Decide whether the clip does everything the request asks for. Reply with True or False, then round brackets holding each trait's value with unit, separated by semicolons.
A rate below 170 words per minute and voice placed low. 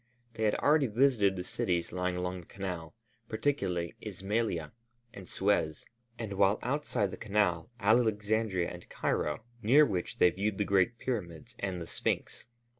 True (150 wpm; 100 Hz)